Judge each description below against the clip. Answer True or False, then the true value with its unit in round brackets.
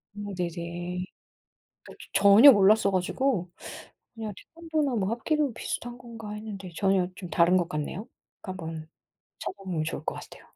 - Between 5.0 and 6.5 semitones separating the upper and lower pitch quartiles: False (4.2 semitones)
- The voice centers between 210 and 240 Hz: False (200 Hz)